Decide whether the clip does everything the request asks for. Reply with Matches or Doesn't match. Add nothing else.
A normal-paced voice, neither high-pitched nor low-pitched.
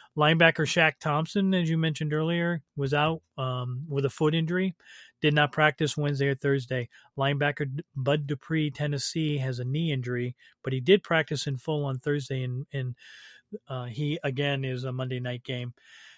Matches